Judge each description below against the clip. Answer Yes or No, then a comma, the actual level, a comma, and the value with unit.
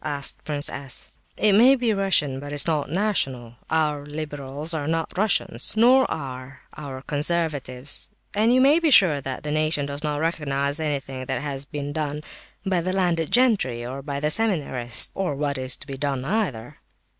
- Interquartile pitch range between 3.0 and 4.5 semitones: Yes, average, 4.1 semitones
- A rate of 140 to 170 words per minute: No, average, 180 wpm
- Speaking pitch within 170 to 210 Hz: No, medium, 150 Hz